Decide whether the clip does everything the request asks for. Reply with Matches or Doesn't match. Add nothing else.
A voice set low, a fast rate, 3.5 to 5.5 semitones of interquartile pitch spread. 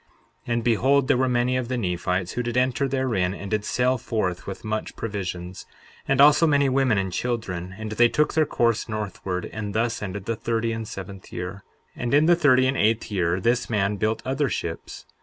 Matches